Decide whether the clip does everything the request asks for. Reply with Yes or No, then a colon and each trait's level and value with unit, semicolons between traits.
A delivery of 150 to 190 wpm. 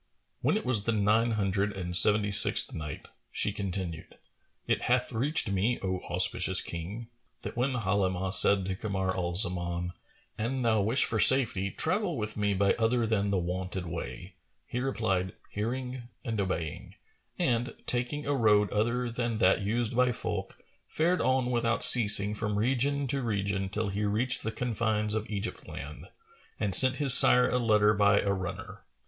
Yes: average, 165 wpm